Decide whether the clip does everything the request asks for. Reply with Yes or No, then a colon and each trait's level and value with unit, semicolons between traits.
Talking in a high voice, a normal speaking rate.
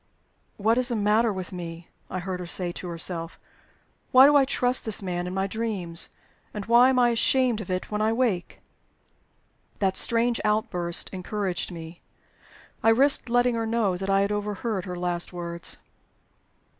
Yes: high, 205 Hz; average, 170 wpm